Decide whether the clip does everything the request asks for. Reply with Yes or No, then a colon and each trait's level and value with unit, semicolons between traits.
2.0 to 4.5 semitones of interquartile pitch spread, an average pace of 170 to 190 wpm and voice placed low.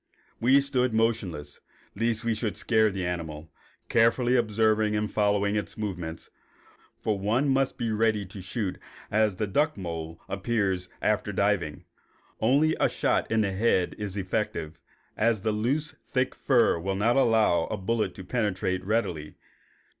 No: average, 3.5 semitones; average, 155 wpm; low, 105 Hz